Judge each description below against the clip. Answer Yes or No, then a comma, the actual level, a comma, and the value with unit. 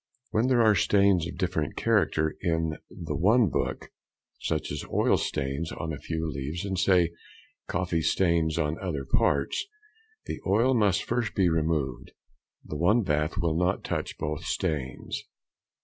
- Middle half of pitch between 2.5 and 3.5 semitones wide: No, average, 3.9 semitones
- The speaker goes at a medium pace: Yes, average, 150 wpm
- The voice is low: Yes, very low, 85 Hz